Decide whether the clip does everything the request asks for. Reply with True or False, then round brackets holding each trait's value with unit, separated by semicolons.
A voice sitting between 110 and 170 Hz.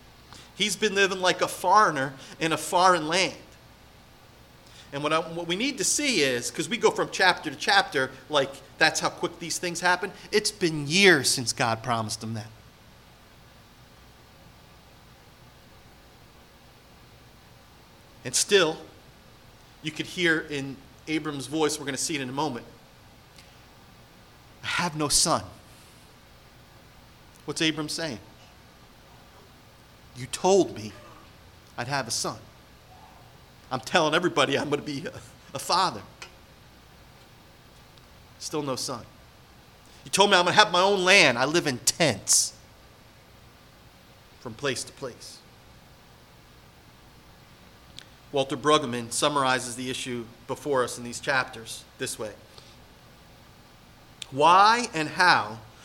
True (140 Hz)